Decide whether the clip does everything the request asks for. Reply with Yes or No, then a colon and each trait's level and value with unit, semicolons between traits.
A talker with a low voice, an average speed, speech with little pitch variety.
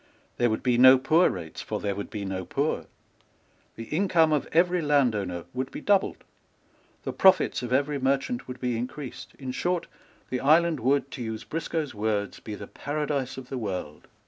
No: low, 130 Hz; average, 180 wpm; average, 5.3 semitones